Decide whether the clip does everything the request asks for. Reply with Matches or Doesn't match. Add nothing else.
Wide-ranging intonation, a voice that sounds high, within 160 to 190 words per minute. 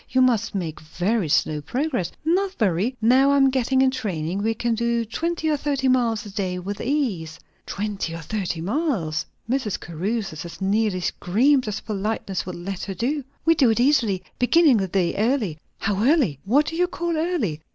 Matches